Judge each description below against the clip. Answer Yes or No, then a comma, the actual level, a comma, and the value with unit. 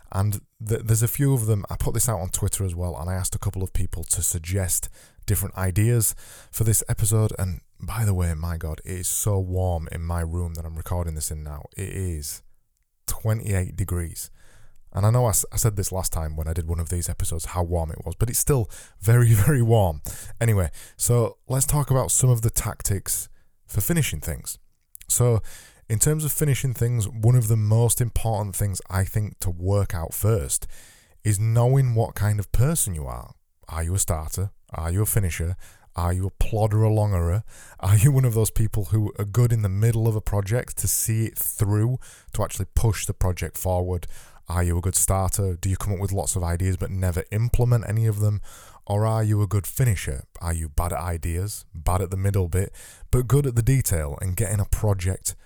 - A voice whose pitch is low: Yes, low, 100 Hz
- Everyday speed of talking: No, fast, 215 wpm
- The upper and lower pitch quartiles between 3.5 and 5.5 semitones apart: Yes, average, 4.0 semitones